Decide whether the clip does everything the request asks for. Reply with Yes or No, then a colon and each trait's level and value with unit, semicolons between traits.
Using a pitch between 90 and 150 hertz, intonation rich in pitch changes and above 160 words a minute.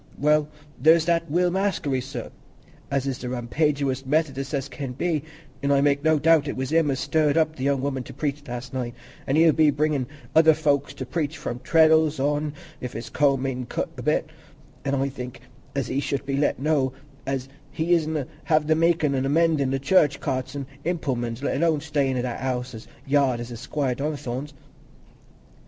No: medium, 140 Hz; average, 2.9 semitones; average, 200 wpm